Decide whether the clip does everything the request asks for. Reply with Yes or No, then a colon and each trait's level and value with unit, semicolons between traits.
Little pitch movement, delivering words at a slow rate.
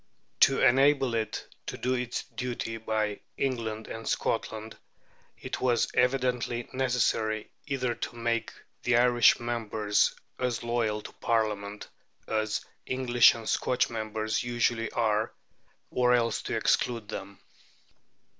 Yes: narrow, 2.1 semitones; slow, 120 wpm